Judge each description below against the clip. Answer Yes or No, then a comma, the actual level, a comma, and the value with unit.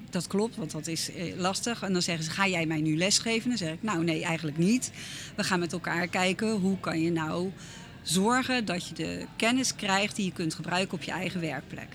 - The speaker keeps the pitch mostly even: No, average, 3.4 semitones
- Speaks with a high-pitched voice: No, medium, 180 Hz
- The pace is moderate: No, fast, 225 wpm